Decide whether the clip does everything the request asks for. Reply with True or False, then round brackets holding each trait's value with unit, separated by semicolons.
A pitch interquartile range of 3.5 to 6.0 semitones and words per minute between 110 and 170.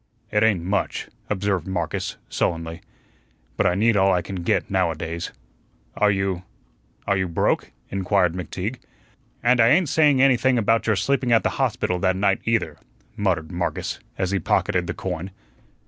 True (4.1 semitones; 165 wpm)